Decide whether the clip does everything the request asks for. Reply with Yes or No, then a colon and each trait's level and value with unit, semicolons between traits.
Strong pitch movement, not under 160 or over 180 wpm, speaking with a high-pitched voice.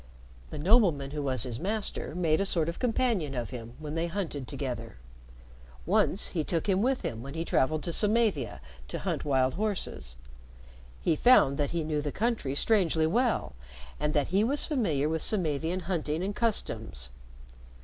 No: wide, 6.4 semitones; average, 170 wpm; medium, 160 Hz